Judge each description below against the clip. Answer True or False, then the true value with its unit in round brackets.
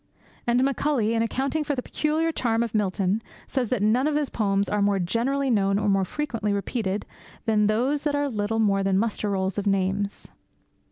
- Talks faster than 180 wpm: True (190 wpm)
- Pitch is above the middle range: True (220 Hz)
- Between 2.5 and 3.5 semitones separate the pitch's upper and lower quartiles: False (4.9 semitones)